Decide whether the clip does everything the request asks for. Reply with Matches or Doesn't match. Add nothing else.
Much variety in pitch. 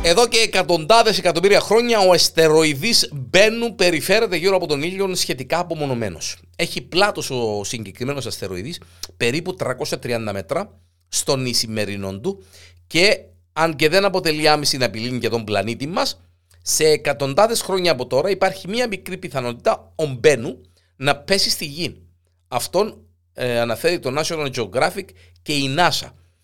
Matches